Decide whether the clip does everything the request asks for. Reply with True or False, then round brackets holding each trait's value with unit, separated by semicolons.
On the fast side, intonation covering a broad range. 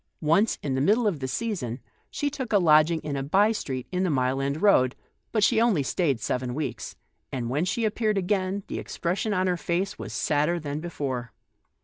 True (210 wpm; 6.6 semitones)